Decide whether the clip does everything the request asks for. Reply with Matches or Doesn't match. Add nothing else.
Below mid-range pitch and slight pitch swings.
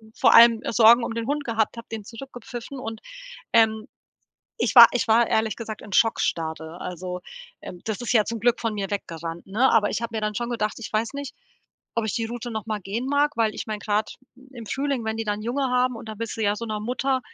Doesn't match